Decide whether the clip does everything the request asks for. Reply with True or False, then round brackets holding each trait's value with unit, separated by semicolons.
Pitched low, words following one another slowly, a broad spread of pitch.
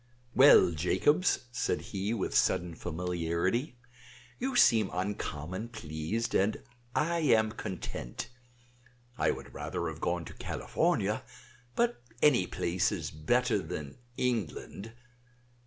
True (100 Hz; 110 wpm; 6.0 semitones)